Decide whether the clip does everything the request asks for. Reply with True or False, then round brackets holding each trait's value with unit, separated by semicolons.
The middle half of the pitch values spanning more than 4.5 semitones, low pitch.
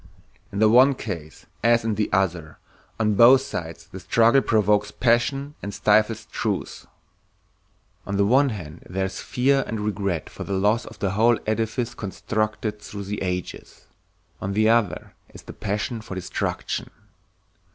False (3.1 semitones; 105 Hz)